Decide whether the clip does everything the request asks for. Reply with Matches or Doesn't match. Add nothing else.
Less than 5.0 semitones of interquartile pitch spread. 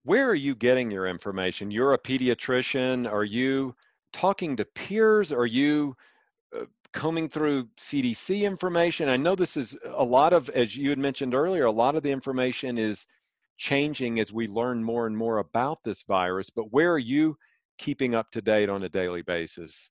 Doesn't match